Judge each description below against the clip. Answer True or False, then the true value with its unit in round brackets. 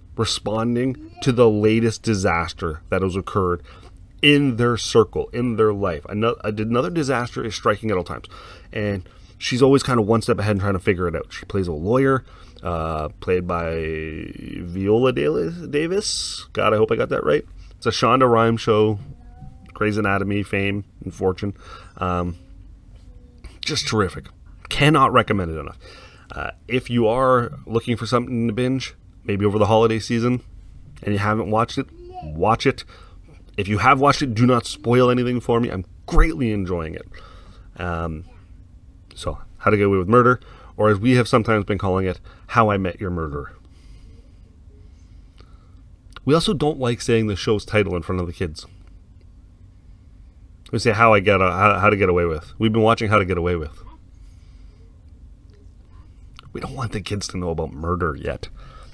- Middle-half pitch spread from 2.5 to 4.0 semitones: False (4.7 semitones)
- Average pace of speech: True (170 wpm)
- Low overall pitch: True (100 Hz)